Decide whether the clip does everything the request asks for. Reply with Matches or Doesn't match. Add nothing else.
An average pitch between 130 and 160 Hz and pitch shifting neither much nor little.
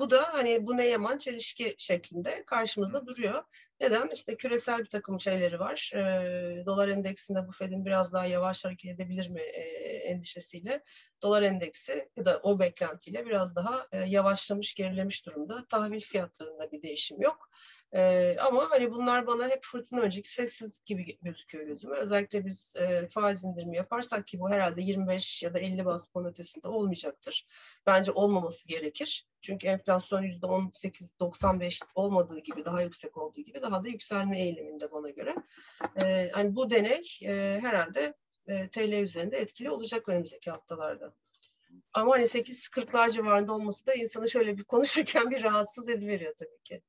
Doesn't match